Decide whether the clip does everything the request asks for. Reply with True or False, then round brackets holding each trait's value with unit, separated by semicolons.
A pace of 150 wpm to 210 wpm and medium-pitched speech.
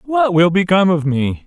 True (205 wpm; 180 Hz)